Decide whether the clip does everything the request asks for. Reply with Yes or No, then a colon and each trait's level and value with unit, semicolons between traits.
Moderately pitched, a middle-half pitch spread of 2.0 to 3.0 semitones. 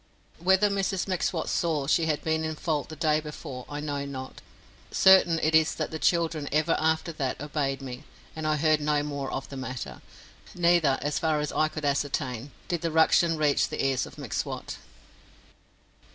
Yes: medium, 155 Hz; narrow, 2.4 semitones